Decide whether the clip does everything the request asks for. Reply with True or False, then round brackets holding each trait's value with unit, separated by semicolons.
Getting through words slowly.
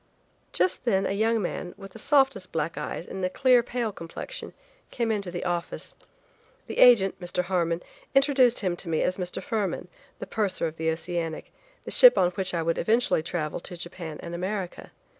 False (185 wpm)